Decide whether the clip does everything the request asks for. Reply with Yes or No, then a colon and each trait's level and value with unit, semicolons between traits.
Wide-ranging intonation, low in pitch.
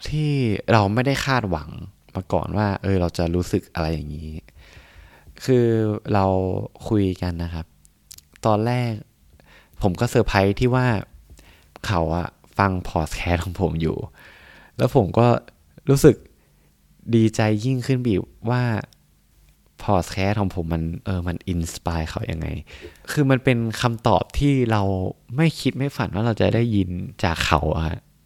Yes: wide, 5.9 semitones; very low, 95 Hz